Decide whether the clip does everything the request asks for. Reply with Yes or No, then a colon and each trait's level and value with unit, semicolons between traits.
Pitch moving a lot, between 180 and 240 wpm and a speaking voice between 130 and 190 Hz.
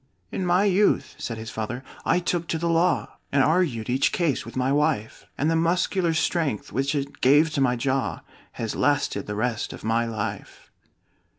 Yes: wide, 6.0 semitones; average, 185 wpm; medium, 140 Hz